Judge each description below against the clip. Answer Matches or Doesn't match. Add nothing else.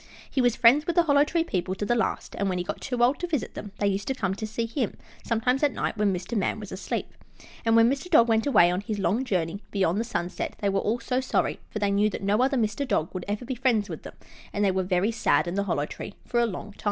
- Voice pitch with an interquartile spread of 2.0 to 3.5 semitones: Doesn't match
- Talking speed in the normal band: Doesn't match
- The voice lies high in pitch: Matches